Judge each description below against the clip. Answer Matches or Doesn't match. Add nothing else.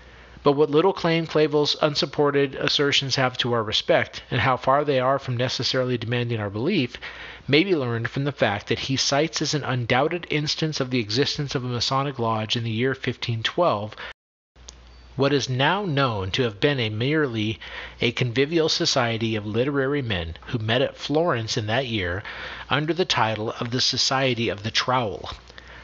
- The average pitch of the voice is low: Matches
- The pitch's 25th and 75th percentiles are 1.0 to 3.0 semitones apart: Doesn't match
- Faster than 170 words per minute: Matches